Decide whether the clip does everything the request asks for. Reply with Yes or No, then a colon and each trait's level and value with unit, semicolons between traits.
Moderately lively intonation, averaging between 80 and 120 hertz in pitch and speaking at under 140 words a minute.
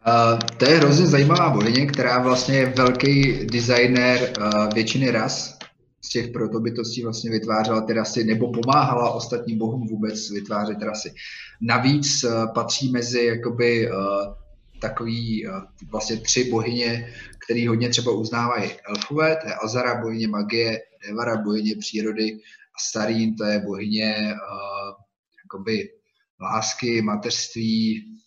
No: narrow, 2.3 semitones; low, 115 Hz; average, 130 wpm